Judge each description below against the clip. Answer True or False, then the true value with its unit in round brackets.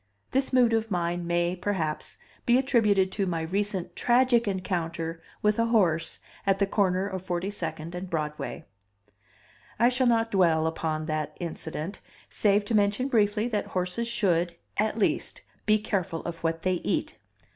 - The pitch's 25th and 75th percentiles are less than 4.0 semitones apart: False (4.3 semitones)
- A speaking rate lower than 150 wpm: False (155 wpm)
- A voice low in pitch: False (190 Hz)